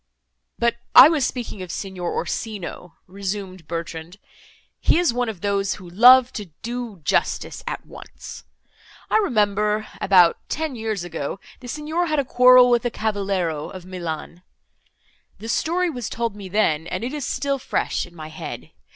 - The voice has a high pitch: Yes, high, 210 Hz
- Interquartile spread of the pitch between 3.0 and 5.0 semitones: No, wide, 5.4 semitones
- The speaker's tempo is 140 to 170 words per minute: Yes, average, 160 wpm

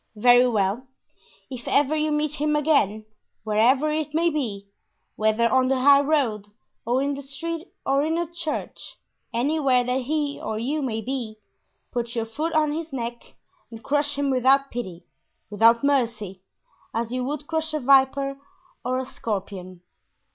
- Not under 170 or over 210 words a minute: No, average, 160 wpm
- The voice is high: Yes, very high, 265 Hz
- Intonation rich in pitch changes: No, average, 4.3 semitones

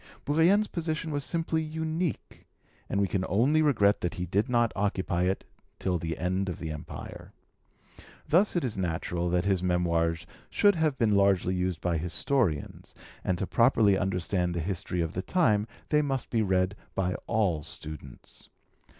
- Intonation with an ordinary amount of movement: No, wide, 7.6 semitones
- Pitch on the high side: No, low, 100 Hz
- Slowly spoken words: No, average, 165 wpm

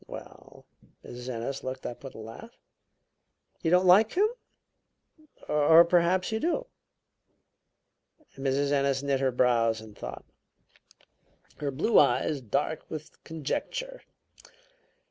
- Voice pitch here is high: No, medium, 140 Hz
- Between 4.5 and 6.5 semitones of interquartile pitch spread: Yes, wide, 5.6 semitones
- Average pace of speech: No, slow, 120 wpm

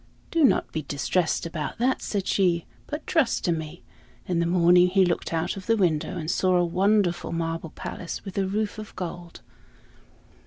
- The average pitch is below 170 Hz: No, medium, 180 Hz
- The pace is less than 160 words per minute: No, average, 185 wpm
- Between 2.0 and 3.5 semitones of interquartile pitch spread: Yes, average, 2.8 semitones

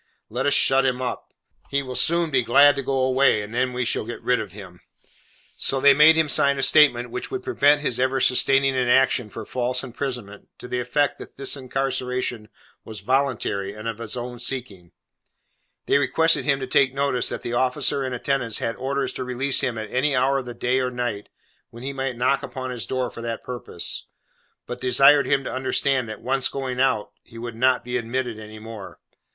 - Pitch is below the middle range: Yes, low, 130 Hz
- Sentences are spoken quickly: Yes, fast, 210 wpm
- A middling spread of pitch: No, narrow, 2.3 semitones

